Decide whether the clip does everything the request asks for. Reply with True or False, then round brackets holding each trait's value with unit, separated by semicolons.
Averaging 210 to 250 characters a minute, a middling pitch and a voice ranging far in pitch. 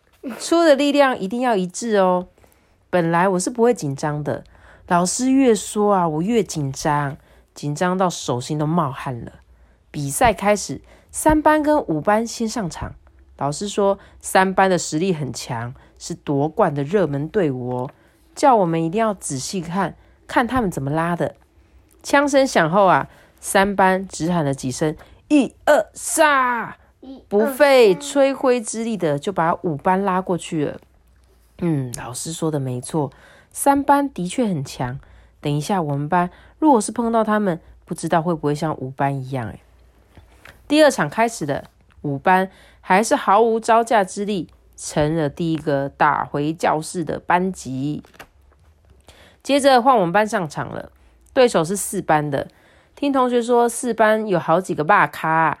True (225 characters per minute; 175 Hz; 7.5 semitones)